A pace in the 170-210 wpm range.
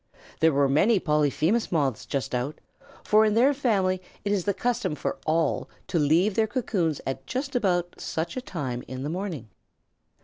Yes: average, 175 wpm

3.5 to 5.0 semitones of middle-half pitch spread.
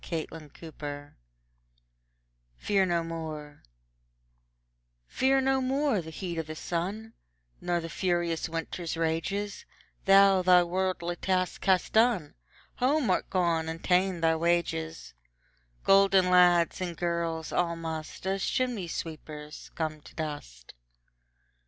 No: average, 2.8 semitones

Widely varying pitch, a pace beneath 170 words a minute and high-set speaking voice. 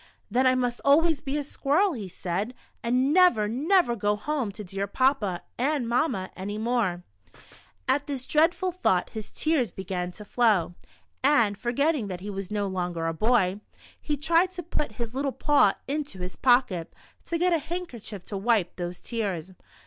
No: wide, 6.8 semitones; average, 180 wpm; high, 240 Hz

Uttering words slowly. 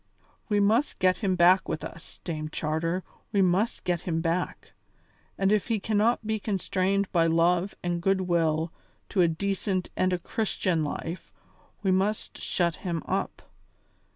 No: average, 155 wpm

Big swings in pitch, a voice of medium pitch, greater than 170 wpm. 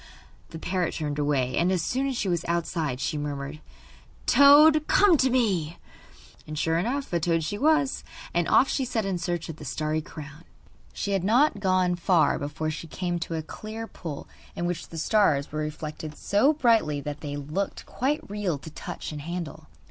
Yes: wide, 5.7 semitones; medium, 170 Hz; average, 190 wpm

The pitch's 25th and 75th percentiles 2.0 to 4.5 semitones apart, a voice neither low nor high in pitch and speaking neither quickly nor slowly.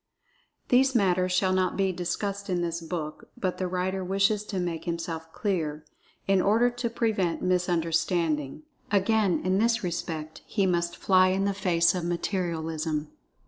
Yes: narrow, 2.6 semitones; medium, 180 Hz; average, 150 wpm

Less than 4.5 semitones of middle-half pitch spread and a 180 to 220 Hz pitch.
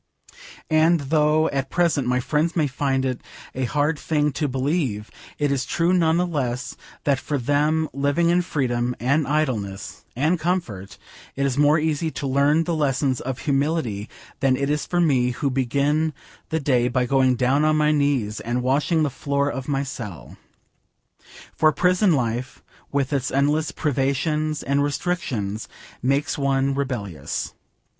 No: average, 3.2 semitones; medium, 140 Hz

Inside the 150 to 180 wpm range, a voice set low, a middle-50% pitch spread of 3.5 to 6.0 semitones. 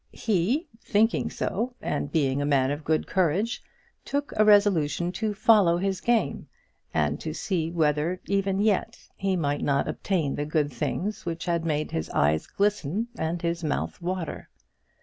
No: average, 160 wpm; medium, 175 Hz; average, 5.2 semitones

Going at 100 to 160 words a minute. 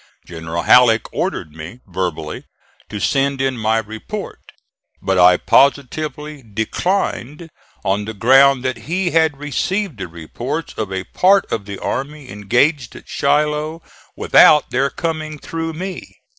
Yes: slow, 135 wpm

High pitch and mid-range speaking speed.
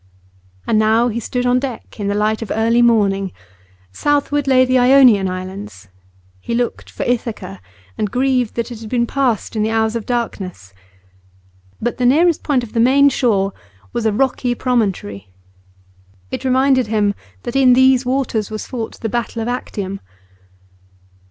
Yes: high, 235 Hz; average, 165 wpm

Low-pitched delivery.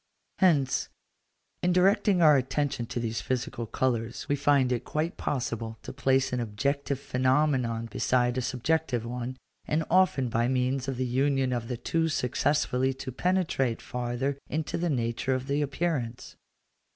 Yes: low, 130 Hz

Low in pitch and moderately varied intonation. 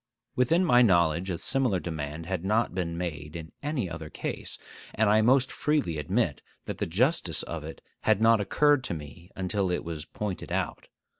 No: very low, 95 Hz; wide, 6.2 semitones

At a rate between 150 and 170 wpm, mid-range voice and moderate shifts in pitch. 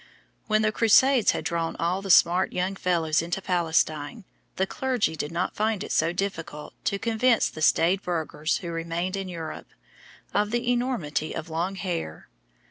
Yes: average, 165 wpm; medium, 180 Hz; average, 4.3 semitones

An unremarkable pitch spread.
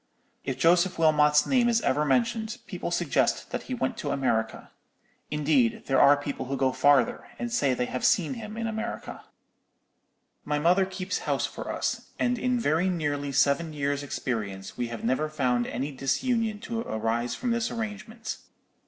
No: wide, 8.6 semitones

